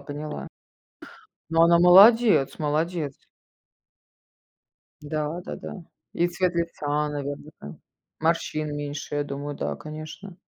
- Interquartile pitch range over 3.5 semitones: No, average, 2.7 semitones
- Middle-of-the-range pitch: Yes, medium, 155 Hz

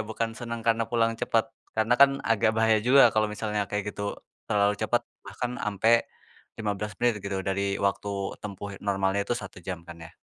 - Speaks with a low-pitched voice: Yes, low, 105 Hz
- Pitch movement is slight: Yes, narrow, 2.2 semitones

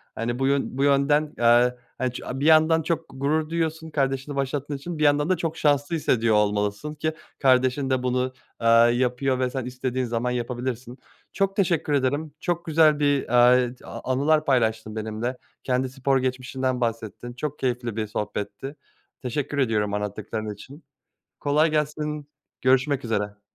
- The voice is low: Yes, low, 130 Hz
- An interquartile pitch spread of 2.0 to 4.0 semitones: Yes, average, 3.5 semitones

